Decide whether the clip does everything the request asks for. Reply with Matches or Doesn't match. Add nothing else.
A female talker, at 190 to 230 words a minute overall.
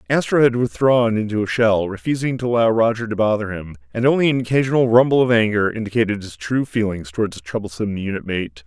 Doesn't match